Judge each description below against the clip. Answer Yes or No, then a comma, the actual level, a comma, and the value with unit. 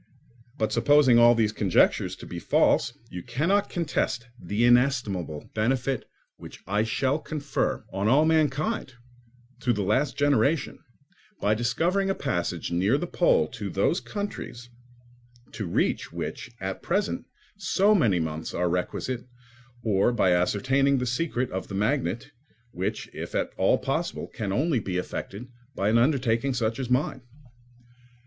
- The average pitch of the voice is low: Yes, low, 120 Hz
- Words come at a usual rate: Yes, average, 145 wpm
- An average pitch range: No, wide, 5.8 semitones